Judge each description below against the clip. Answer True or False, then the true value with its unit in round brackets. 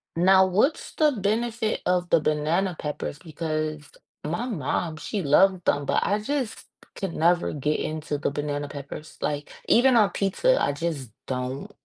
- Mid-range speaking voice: True (170 Hz)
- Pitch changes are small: False (5.3 semitones)